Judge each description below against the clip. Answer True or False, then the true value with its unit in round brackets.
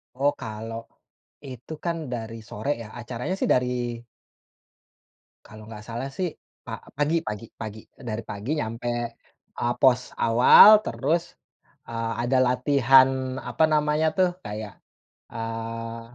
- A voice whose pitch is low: True (125 Hz)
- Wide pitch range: False (3.9 semitones)